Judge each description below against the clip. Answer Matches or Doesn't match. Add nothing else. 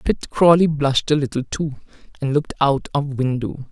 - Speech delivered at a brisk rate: Doesn't match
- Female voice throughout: Matches